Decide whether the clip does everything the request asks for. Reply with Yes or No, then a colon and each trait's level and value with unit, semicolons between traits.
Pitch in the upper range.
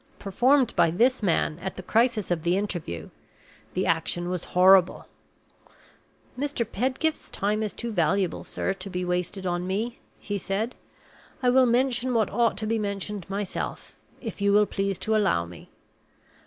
Yes: high, 200 Hz